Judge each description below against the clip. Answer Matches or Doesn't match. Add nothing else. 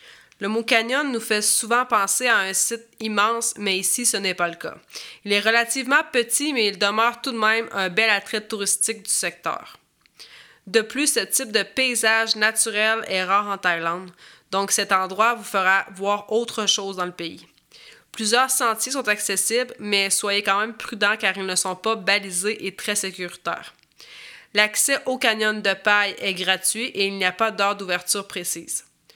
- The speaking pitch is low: Doesn't match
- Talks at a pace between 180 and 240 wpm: Matches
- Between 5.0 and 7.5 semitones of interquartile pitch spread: Doesn't match